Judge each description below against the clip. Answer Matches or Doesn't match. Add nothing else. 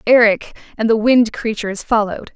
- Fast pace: Doesn't match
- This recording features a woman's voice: Matches